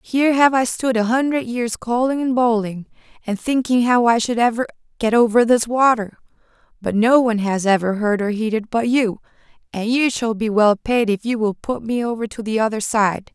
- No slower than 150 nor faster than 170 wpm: No, fast, 205 wpm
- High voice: Yes, high, 230 Hz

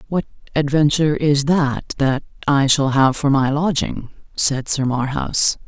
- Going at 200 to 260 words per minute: No, average, 150 wpm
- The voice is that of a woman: Yes, female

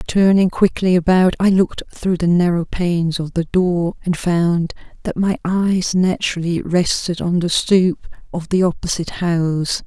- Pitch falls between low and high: Yes, medium, 175 Hz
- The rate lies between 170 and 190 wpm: No, average, 160 wpm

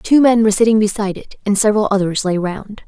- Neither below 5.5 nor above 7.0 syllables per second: Yes, 6.5 syllables/s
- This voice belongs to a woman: Yes, female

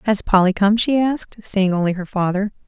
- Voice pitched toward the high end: Yes, high, 200 Hz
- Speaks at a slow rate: No, average, 200 wpm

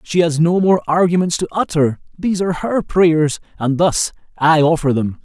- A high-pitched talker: No, medium, 165 Hz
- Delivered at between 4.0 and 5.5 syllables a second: Yes, 4.9 syllables/s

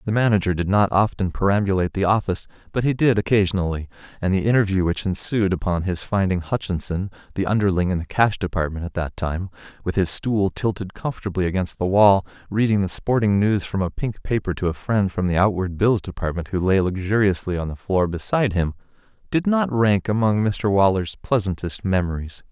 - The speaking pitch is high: No, very low, 95 Hz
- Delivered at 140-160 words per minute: No, average, 185 wpm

